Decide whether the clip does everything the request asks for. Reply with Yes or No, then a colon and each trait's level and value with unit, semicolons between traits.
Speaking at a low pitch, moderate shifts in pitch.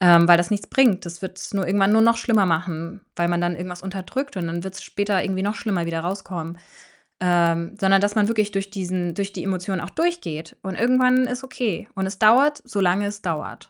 No: high, 190 Hz; average, 3.2 semitones